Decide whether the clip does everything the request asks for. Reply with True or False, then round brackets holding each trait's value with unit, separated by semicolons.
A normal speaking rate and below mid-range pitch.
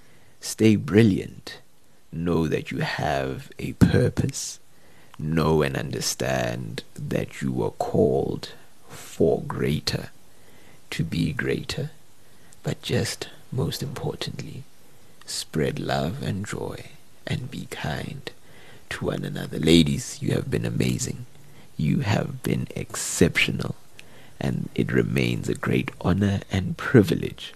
False (110 wpm; 85 Hz)